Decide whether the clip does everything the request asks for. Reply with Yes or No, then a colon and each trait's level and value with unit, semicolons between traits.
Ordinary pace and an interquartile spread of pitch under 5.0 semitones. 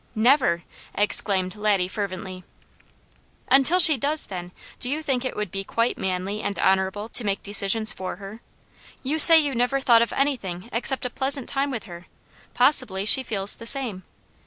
No: average, 170 wpm; wide, 5.6 semitones